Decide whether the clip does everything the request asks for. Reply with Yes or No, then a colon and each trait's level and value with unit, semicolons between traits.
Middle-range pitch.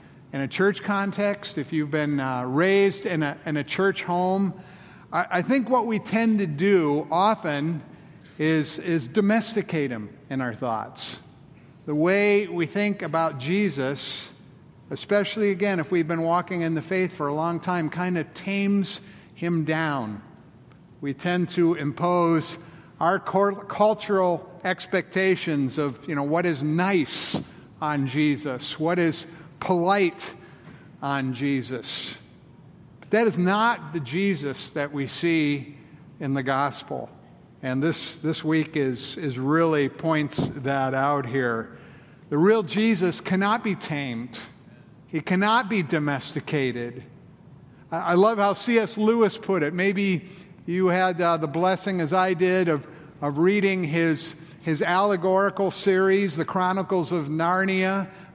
Yes: medium, 170 Hz